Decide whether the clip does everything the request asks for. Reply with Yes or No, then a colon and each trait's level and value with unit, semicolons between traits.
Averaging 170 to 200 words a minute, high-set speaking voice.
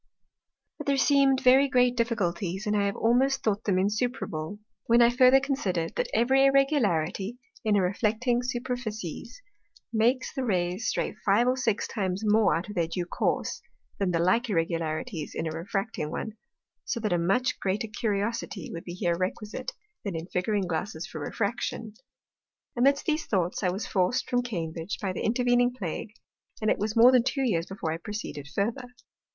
Yes: average, 175 wpm; high, 210 Hz